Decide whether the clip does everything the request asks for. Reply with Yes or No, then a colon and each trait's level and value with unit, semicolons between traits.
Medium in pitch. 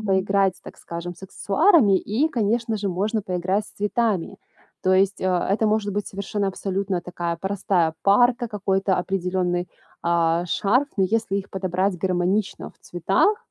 No: high, 195 Hz